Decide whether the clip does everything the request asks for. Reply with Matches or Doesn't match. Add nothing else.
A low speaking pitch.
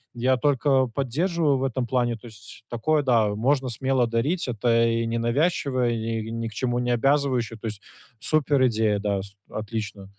Matches